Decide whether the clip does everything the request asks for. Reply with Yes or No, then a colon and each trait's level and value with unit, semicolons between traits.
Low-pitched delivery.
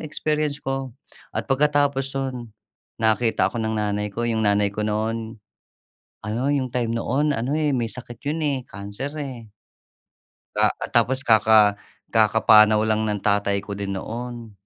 Yes: low, 115 Hz